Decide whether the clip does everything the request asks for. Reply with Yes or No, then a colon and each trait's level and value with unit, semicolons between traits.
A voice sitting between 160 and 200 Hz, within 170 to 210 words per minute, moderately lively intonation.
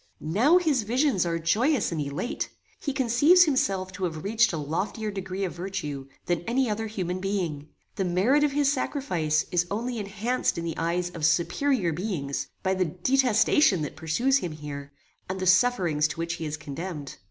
No: high, 190 Hz; average, 180 wpm; wide, 6.5 semitones